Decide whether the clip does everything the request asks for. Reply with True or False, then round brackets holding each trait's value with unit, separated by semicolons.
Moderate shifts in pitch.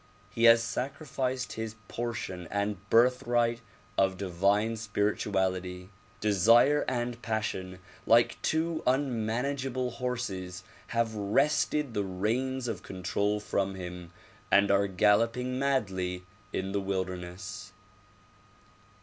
True (4.3 semitones)